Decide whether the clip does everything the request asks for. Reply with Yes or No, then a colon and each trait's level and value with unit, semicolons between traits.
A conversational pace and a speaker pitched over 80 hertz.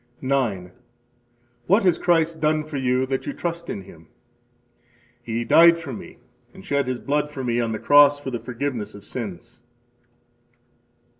Yes: average, 160 wpm; low, 135 Hz